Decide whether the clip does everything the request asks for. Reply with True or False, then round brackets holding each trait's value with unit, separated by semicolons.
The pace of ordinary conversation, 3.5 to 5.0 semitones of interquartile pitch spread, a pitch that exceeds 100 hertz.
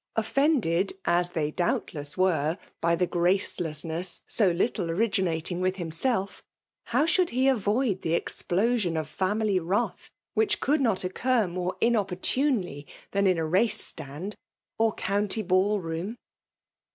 False (130 wpm; 4.6 semitones; 185 Hz)